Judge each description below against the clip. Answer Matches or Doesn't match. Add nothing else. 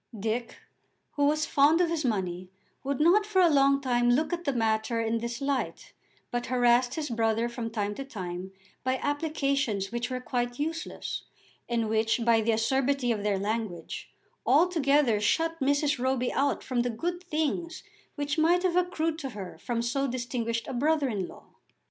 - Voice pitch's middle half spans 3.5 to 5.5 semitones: Matches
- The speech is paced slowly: Doesn't match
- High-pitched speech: Matches